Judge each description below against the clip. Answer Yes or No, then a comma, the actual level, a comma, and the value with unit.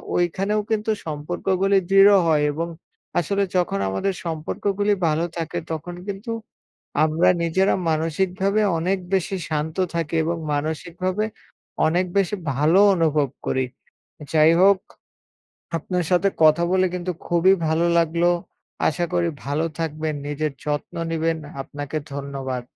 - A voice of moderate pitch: Yes, medium, 170 Hz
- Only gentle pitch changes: No, average, 3.4 semitones